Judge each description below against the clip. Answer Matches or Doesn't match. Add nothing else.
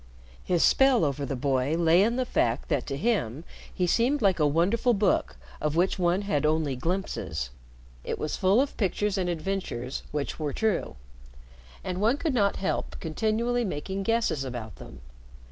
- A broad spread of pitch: Matches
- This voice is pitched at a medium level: Matches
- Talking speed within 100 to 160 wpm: Doesn't match